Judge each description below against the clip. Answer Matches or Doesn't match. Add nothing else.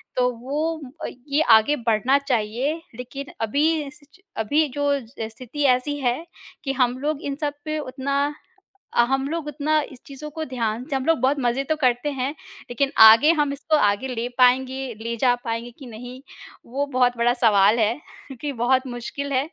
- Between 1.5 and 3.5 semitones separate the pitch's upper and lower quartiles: Matches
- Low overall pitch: Doesn't match